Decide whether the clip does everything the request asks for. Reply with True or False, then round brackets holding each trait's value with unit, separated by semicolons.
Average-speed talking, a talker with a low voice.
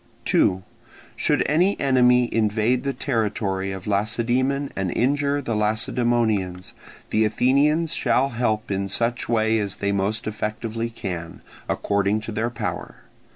False (130 wpm; 115 Hz)